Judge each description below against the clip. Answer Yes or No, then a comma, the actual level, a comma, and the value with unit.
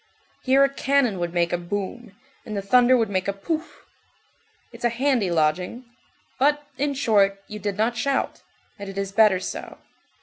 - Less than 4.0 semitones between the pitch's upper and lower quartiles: No, average, 4.8 semitones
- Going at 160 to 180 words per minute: Yes, average, 175 wpm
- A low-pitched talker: No, high, 215 Hz